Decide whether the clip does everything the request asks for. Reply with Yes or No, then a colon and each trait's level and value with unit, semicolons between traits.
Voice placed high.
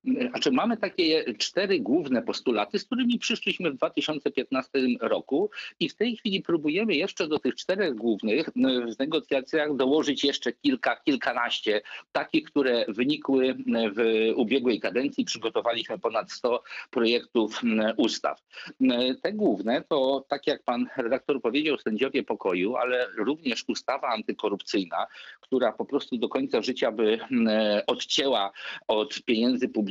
No: low, 135 Hz